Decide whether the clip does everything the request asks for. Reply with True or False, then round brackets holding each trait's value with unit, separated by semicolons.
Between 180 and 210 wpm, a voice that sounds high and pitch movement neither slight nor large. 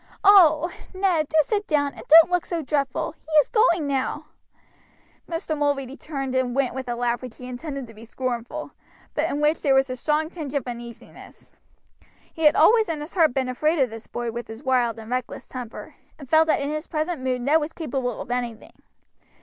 True (205 wpm; 280 Hz; 4.0 semitones)